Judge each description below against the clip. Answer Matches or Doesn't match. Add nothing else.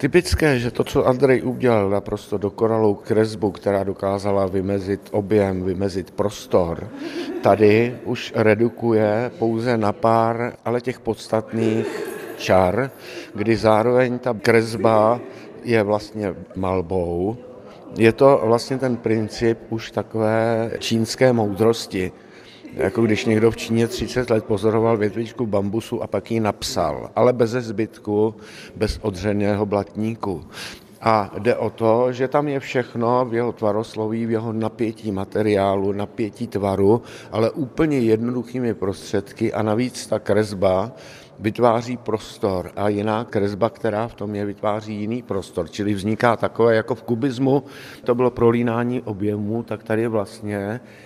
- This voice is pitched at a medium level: Doesn't match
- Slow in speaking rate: Doesn't match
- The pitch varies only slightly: Matches